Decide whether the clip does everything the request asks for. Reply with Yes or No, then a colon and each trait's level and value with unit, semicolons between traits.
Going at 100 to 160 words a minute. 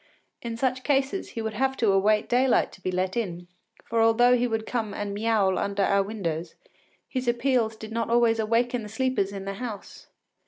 No: average, 195 wpm